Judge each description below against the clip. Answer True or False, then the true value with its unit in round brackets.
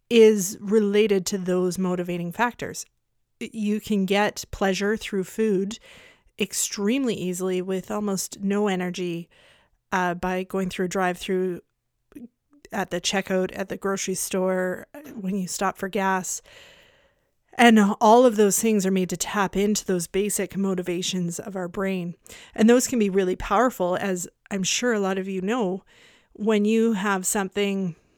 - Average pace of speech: True (150 wpm)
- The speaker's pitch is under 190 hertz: False (195 Hz)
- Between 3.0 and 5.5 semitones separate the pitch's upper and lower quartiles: False (2.5 semitones)